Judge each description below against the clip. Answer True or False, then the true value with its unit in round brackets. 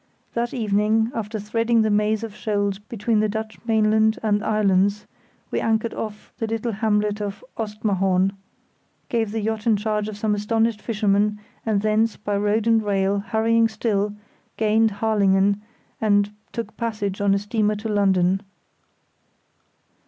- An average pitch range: False (1.5 semitones)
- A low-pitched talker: False (210 Hz)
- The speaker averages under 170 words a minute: True (155 wpm)